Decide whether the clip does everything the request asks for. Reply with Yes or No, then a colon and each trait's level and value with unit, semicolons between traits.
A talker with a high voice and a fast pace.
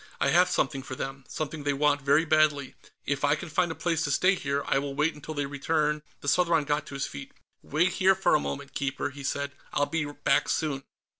No: medium, 145 Hz; fast, 235 wpm